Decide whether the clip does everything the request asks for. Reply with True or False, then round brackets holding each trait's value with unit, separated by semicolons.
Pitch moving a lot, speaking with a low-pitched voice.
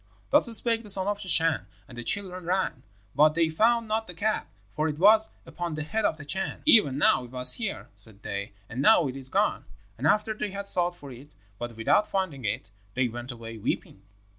False (8.2 semitones; 160 Hz)